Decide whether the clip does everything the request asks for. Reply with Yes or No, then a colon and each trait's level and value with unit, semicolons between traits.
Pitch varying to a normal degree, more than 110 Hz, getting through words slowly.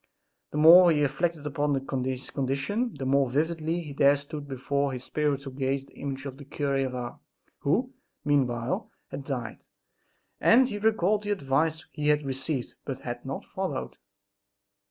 No: average, 3.1 semitones; medium, 140 Hz; average, 155 wpm